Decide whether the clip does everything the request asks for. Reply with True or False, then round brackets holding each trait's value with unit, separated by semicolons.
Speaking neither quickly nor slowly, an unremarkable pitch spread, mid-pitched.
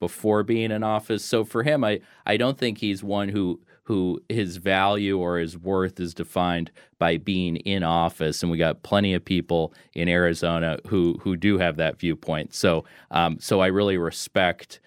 False (185 wpm; 3.1 semitones; 90 Hz)